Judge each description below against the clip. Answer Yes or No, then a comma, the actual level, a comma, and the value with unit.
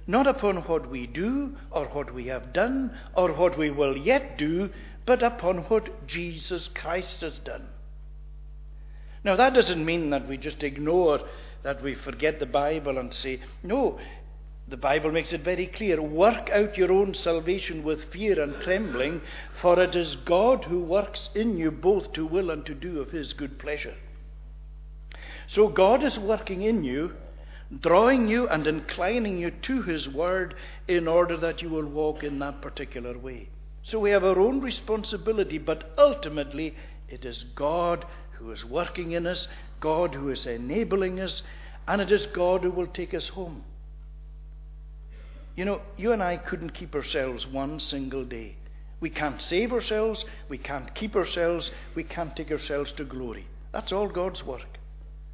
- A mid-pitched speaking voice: Yes, medium, 165 Hz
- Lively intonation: Yes, wide, 5.7 semitones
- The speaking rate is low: No, average, 170 wpm